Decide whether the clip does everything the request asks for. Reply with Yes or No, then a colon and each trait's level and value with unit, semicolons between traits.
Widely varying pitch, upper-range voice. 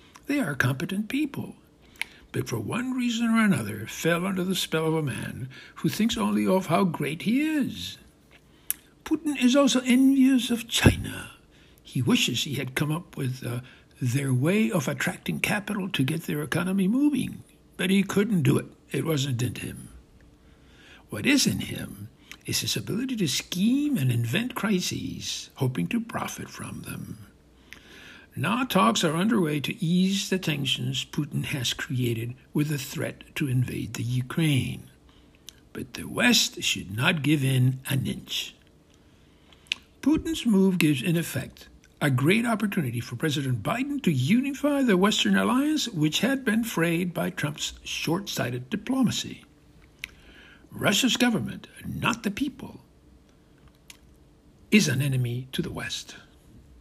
No: wide, 8.7 semitones; medium, 170 Hz